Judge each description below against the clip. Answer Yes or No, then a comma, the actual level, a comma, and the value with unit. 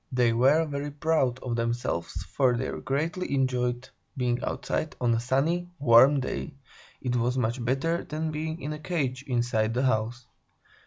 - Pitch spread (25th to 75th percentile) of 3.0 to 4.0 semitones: Yes, average, 3.6 semitones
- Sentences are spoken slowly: No, average, 160 wpm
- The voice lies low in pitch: Yes, low, 130 Hz